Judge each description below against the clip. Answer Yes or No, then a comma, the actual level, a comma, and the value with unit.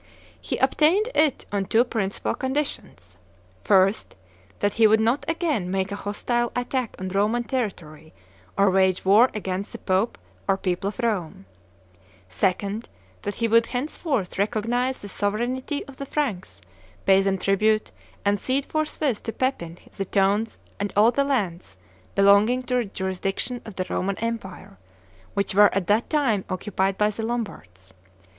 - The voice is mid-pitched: No, high, 210 Hz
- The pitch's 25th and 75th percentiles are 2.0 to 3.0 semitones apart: No, average, 4.1 semitones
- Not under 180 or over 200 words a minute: No, average, 150 wpm